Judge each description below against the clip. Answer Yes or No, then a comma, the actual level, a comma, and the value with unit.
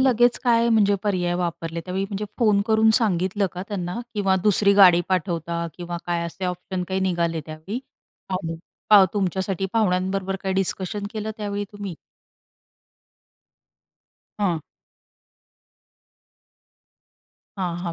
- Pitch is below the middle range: No, high, 190 Hz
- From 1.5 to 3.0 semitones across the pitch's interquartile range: Yes, average, 2.7 semitones